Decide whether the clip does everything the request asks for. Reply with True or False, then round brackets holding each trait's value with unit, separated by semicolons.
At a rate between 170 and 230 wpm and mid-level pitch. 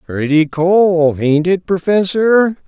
False (110 wpm; 175 Hz)